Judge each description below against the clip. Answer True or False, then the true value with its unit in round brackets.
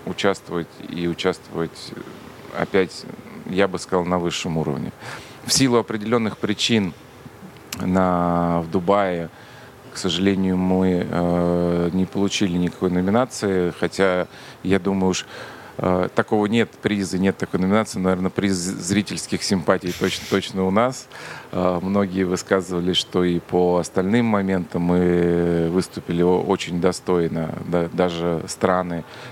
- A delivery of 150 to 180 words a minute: False (120 wpm)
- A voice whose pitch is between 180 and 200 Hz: False (95 Hz)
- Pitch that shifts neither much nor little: False (2.2 semitones)